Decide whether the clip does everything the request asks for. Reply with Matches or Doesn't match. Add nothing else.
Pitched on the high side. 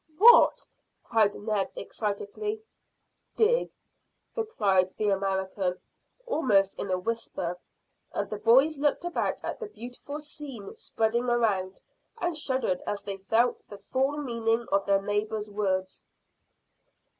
Matches